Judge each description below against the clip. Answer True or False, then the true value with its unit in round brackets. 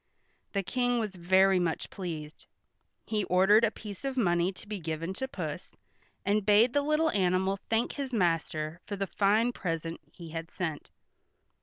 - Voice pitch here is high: True (195 Hz)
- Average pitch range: True (4.4 semitones)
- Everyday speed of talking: True (165 wpm)